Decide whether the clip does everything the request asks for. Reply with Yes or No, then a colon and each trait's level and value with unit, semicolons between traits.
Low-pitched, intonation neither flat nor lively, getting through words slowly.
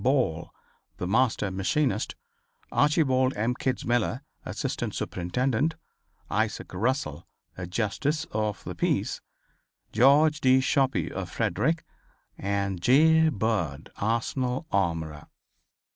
No: low, 120 Hz; wide, 5.9 semitones; slow, 100 wpm